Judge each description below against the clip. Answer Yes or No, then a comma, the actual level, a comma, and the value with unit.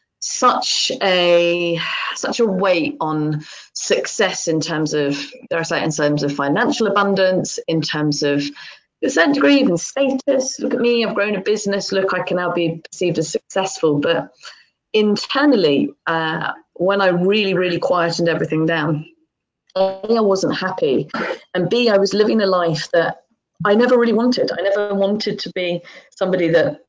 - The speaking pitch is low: No, medium, 185 Hz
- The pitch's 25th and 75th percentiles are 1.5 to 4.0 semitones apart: No, average, 4.4 semitones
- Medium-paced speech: Yes, average, 165 wpm